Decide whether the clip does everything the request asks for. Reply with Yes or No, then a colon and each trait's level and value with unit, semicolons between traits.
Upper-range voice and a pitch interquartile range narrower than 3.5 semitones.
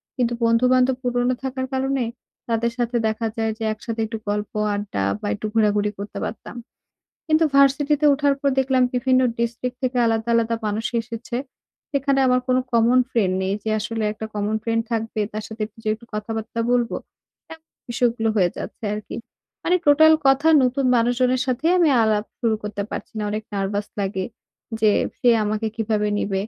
Yes: high, 230 Hz; average, 3.0 semitones